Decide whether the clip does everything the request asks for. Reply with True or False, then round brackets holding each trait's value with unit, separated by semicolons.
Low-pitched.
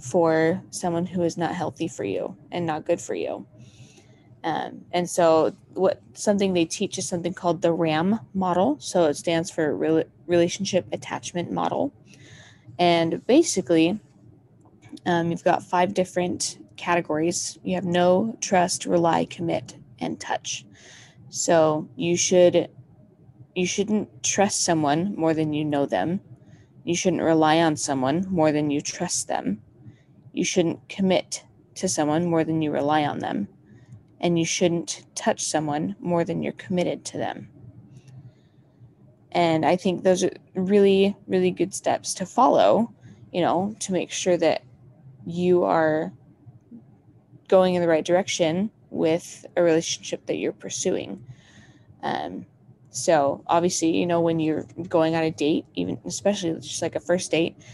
False (170 Hz)